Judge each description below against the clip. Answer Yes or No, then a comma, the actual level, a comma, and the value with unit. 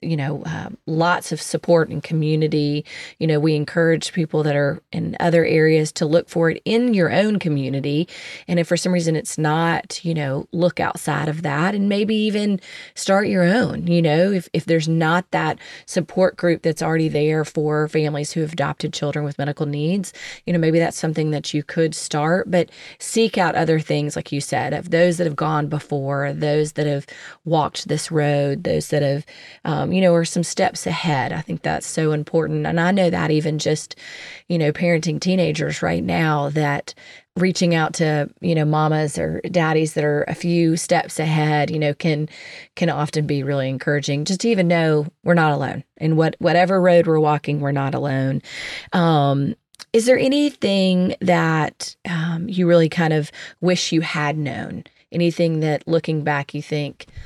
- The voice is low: No, medium, 160 Hz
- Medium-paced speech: Yes, average, 190 wpm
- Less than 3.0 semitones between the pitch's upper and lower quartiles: Yes, narrow, 2.5 semitones